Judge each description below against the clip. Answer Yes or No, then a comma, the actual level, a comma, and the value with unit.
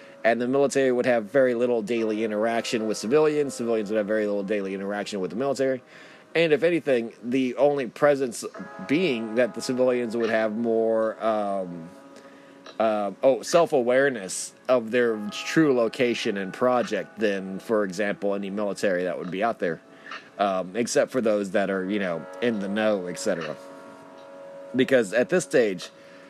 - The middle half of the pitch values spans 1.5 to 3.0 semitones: No, average, 3.7 semitones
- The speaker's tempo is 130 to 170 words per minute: Yes, average, 160 wpm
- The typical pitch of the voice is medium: No, low, 115 Hz